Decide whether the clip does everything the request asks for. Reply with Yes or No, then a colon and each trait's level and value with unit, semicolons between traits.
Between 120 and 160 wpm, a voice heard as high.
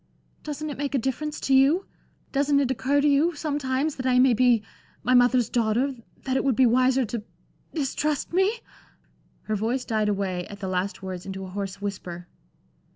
No: average, 185 wpm; very high, 255 Hz